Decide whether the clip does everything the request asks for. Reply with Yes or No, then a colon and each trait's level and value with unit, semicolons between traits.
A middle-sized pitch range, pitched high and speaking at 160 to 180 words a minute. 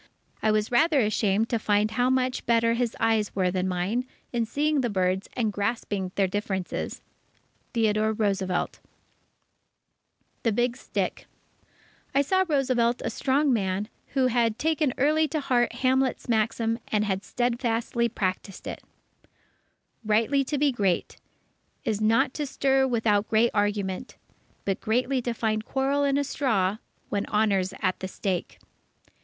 No: average, 3.9 semitones; high, 225 Hz; average, 145 wpm